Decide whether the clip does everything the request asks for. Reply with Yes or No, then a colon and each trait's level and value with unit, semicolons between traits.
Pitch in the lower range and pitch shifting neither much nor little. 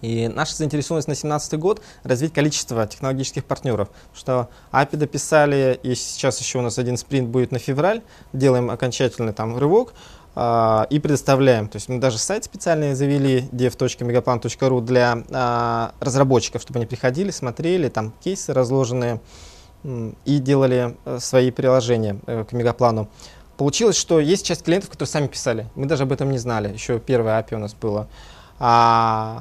Yes: low, 125 Hz; average, 3.2 semitones